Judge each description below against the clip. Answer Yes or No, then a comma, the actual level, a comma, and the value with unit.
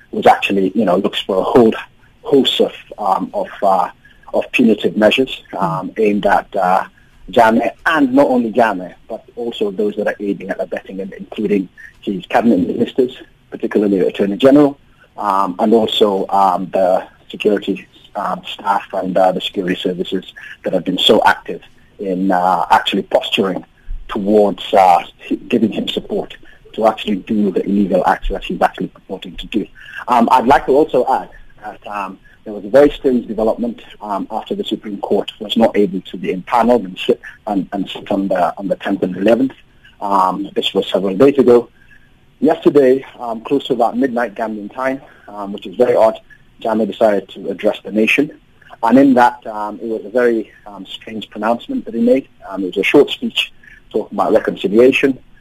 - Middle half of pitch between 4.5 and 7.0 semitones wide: Yes, average, 5.1 semitones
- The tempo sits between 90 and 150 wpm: No, average, 180 wpm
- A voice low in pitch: Yes, low, 120 Hz